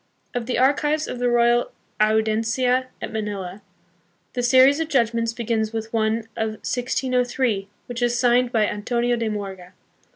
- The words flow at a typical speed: Yes, average, 150 wpm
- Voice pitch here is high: Yes, high, 235 Hz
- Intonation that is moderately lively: No, narrow, 2.3 semitones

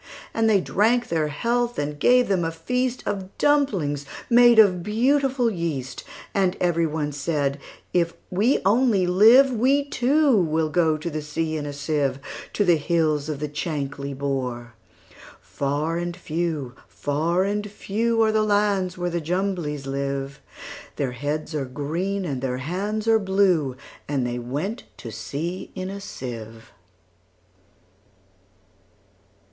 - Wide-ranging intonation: Yes, wide, 6.2 semitones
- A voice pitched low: No, medium, 170 Hz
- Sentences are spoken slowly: Yes, slow, 125 wpm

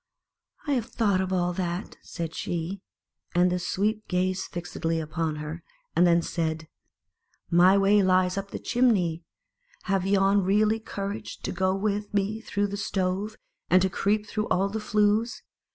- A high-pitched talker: Yes, high, 195 Hz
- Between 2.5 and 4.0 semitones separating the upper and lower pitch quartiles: Yes, average, 2.8 semitones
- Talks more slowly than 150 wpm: No, average, 175 wpm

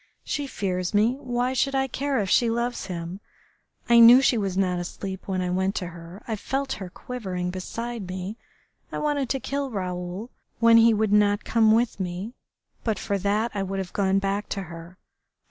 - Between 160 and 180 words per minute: No, average, 195 wpm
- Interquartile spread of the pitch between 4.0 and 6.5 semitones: Yes, average, 4.3 semitones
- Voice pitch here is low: No, high, 205 Hz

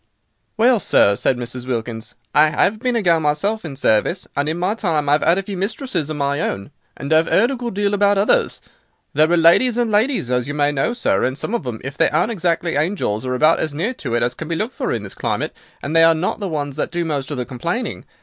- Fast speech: Yes, fast, 255 wpm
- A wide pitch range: Yes, wide, 6.3 semitones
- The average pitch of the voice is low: No, medium, 160 Hz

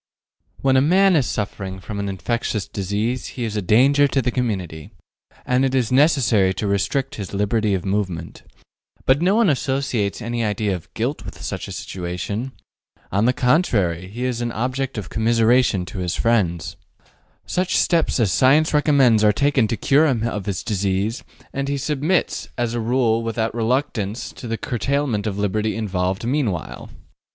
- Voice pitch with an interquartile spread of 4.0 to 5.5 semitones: Yes, average, 4.7 semitones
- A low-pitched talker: Yes, low, 115 Hz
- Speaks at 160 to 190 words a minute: Yes, average, 170 wpm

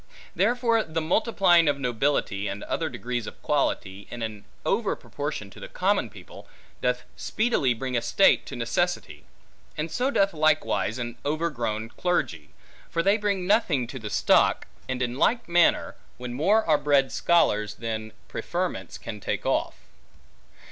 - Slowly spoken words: No, average, 155 wpm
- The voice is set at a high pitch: No, medium, 145 Hz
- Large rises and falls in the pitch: Yes, wide, 7.3 semitones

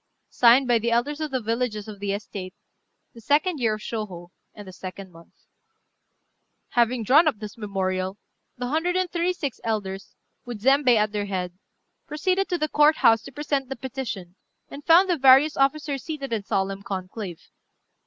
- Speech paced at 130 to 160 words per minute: No, average, 175 wpm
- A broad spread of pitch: Yes, wide, 6.3 semitones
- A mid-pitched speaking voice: No, high, 235 Hz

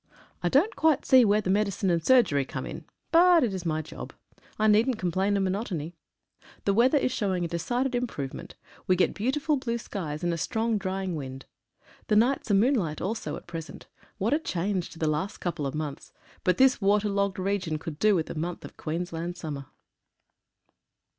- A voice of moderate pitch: No, high, 195 Hz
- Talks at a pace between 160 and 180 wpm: No, average, 195 wpm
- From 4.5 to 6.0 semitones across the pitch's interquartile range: Yes, wide, 5.6 semitones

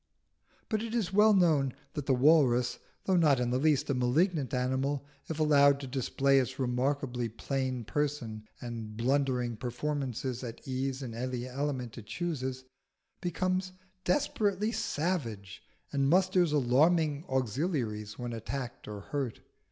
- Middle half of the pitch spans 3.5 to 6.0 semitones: Yes, average, 3.9 semitones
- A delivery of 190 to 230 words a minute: No, slow, 135 wpm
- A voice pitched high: No, low, 135 Hz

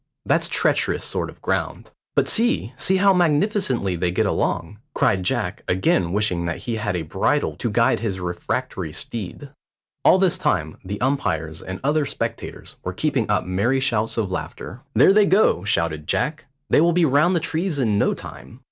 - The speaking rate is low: No, average, 180 wpm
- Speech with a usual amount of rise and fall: No, wide, 8.8 semitones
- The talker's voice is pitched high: No, low, 115 Hz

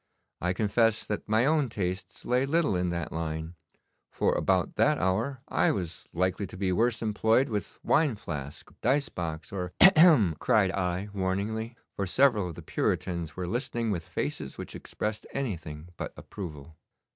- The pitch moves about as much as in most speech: Yes, average, 4.7 semitones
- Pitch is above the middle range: No, low, 100 Hz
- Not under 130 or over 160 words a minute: No, average, 170 wpm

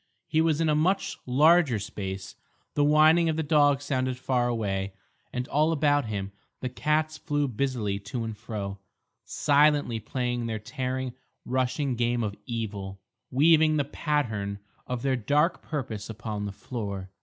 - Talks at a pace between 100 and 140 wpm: No, average, 155 wpm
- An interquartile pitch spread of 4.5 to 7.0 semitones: Yes, wide, 5.4 semitones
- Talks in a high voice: No, low, 130 Hz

